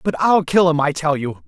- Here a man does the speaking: Yes, male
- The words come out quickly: Yes, fast, 285 wpm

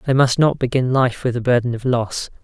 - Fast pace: Yes, fast, 245 wpm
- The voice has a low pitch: Yes, low, 125 Hz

